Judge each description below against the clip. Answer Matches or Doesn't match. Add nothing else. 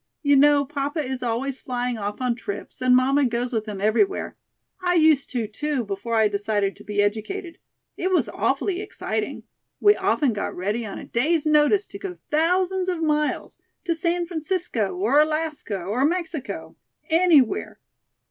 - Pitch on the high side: Matches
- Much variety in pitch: Matches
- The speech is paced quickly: Doesn't match